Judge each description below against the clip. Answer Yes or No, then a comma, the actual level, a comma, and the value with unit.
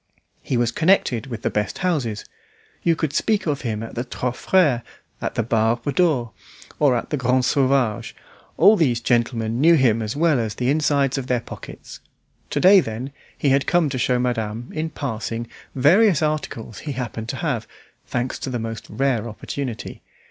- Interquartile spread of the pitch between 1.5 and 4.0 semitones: No, average, 4.4 semitones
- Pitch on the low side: Yes, low, 125 Hz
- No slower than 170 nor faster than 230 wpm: Yes, average, 180 wpm